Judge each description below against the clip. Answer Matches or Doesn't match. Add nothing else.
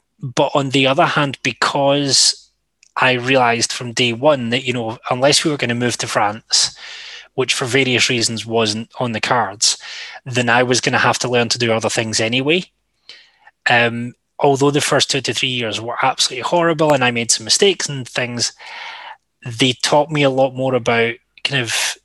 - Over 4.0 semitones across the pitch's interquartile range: Doesn't match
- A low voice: Matches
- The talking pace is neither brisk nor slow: Matches